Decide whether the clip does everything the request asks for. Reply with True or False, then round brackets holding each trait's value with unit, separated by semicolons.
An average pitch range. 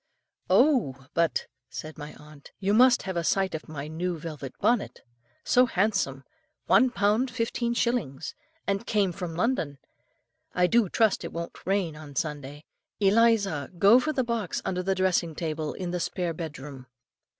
False (6.1 semitones)